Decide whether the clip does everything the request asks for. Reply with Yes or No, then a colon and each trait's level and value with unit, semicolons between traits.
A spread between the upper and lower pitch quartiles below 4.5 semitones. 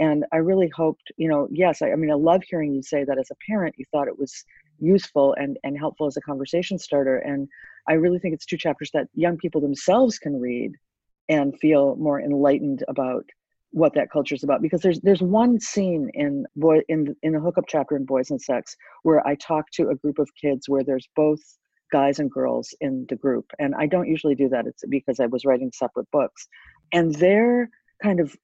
Yes: average, 3.8 semitones